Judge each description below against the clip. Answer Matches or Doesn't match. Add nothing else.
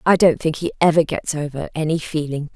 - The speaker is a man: Doesn't match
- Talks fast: Matches